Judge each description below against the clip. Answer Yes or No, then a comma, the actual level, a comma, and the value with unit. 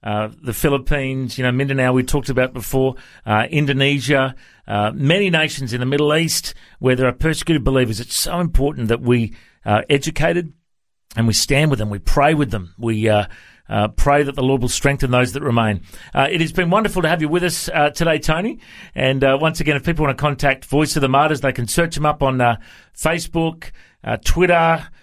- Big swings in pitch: No, average, 4.1 semitones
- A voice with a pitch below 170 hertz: Yes, medium, 140 Hz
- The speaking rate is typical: No, fast, 215 wpm